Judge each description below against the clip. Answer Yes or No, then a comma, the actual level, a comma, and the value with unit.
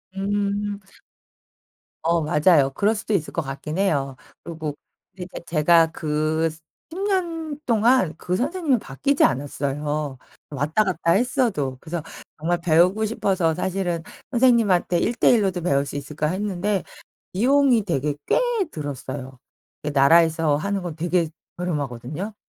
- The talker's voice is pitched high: No, medium, 175 Hz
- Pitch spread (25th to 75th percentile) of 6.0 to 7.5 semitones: No, average, 5.3 semitones